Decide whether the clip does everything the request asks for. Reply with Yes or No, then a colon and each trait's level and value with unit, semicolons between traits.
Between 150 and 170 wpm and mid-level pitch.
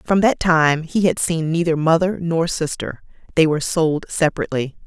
Yes: average, 160 wpm; medium, 165 Hz